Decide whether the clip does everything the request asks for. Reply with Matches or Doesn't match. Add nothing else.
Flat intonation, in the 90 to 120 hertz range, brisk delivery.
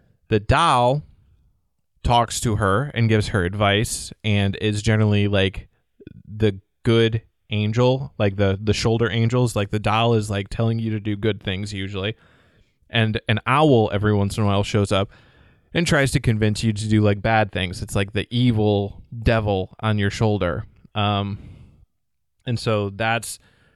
Doesn't match